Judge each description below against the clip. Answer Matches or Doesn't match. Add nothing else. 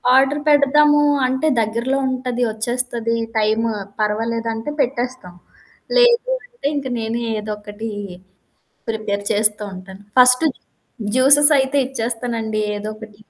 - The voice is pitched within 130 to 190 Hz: Doesn't match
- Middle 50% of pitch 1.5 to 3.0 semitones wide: Doesn't match